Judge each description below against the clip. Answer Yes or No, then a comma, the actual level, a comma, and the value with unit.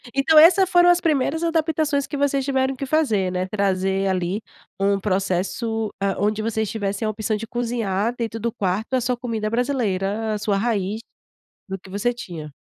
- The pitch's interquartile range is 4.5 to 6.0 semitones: Yes, average, 5.2 semitones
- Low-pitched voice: No, high, 220 Hz